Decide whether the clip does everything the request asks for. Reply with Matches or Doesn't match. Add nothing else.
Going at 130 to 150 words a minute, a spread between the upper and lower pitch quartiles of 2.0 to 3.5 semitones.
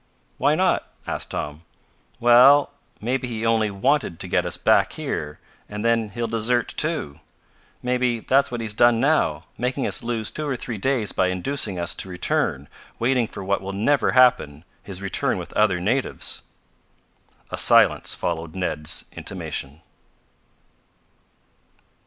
Doesn't match